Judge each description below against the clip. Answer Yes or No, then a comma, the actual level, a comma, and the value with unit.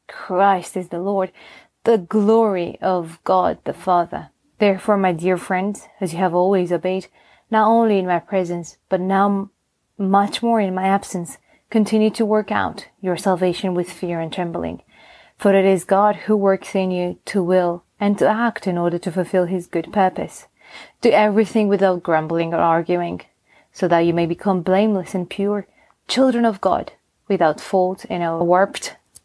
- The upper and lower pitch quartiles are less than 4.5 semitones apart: Yes, narrow, 2.5 semitones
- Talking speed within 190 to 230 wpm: No, average, 170 wpm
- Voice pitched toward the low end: No, high, 190 Hz